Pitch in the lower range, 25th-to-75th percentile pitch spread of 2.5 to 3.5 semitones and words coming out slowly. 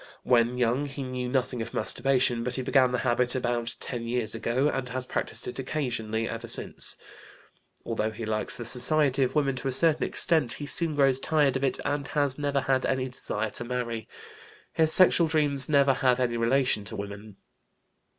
No: low, 125 Hz; average, 2.8 semitones; average, 190 wpm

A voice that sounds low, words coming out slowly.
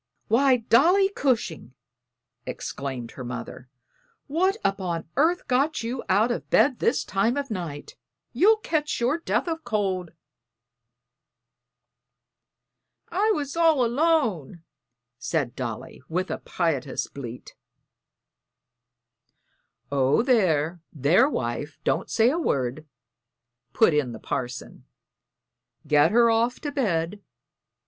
No: high, 215 Hz; slow, 110 wpm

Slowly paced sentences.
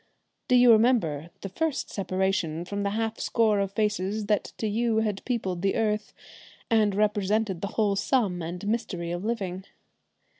No: average, 160 wpm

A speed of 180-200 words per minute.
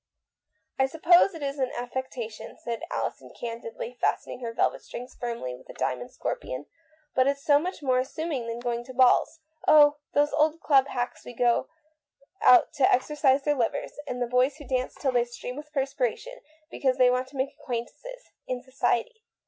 Yes: average, 190 wpm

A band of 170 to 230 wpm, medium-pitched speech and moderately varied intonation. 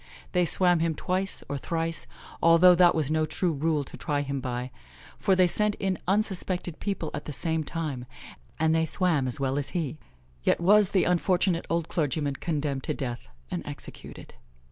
Yes: average, 180 wpm; medium, 165 Hz; average, 3.8 semitones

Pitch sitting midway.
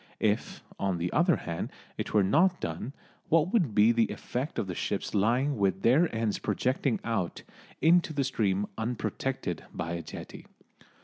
No: low, 115 Hz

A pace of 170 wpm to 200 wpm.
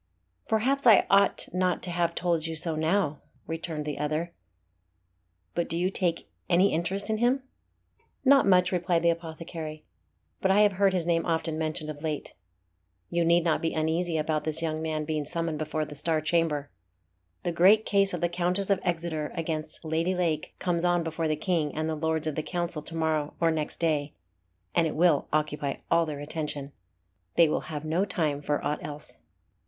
Yes: average, 190 wpm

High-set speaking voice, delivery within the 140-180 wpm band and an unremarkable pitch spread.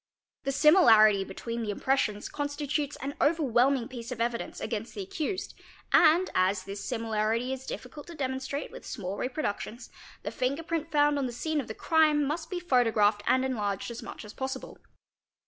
Yes: very high, 260 Hz; average, 175 wpm; average, 4.9 semitones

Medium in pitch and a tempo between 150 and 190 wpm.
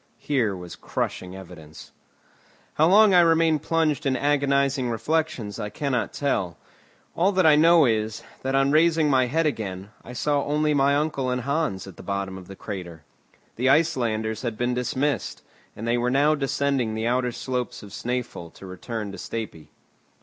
No: low, 125 Hz; average, 170 wpm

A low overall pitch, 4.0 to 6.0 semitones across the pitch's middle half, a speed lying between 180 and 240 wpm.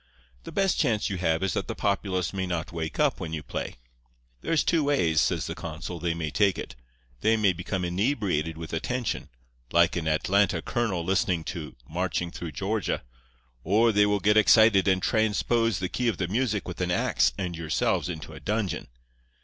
Yes: very low, 95 Hz; average, 4.3 semitones; average, 190 wpm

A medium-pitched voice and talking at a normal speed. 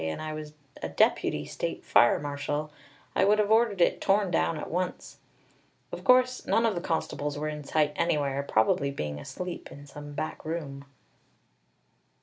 Yes: medium, 150 Hz; average, 165 wpm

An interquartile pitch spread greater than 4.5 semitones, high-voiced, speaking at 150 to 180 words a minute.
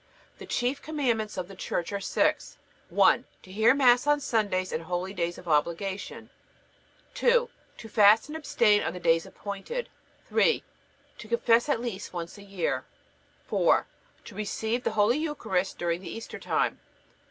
Yes: average, 4.9 semitones; high, 210 Hz; average, 155 wpm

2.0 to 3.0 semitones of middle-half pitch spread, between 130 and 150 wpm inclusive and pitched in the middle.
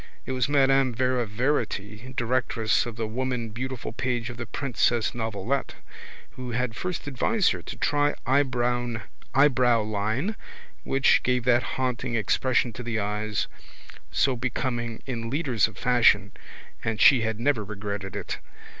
No: average, 2.7 semitones; slow, 135 wpm; low, 120 Hz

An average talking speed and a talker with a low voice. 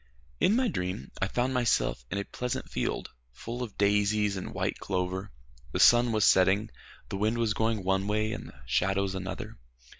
Yes: average, 180 wpm; low, 105 Hz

